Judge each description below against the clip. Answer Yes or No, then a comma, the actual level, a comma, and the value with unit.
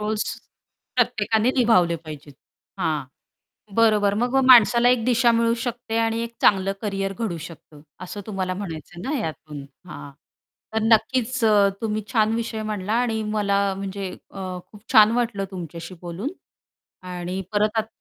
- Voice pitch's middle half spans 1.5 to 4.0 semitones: Yes, average, 3.7 semitones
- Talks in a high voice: Yes, high, 210 Hz